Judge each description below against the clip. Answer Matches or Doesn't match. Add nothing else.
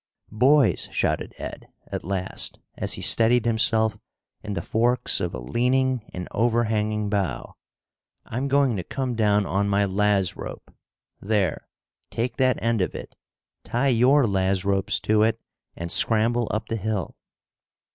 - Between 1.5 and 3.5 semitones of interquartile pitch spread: Matches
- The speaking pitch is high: Doesn't match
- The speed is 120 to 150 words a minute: Matches